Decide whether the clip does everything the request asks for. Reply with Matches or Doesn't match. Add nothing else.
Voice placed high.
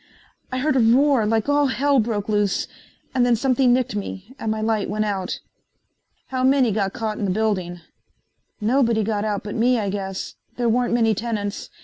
Matches